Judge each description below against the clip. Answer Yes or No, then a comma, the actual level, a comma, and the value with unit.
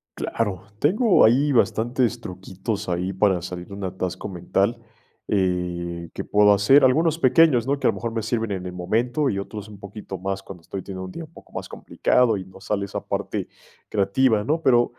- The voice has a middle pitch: No, low, 105 Hz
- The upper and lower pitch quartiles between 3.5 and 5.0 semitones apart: Yes, average, 4.6 semitones